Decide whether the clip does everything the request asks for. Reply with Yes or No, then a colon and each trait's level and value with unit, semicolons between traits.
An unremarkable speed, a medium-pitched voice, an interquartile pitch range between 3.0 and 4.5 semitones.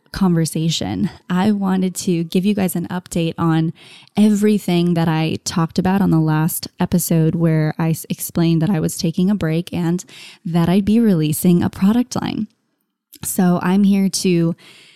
No: average, 160 wpm; medium, 175 Hz; narrow, 2.5 semitones